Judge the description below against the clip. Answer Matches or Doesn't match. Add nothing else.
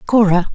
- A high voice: Matches